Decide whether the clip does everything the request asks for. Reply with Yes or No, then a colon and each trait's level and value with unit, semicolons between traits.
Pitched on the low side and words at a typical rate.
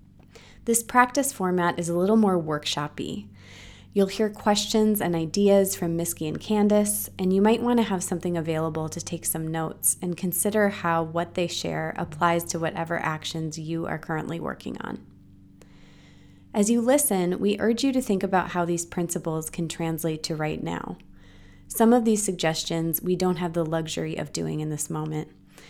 No: medium, 170 Hz; average, 175 wpm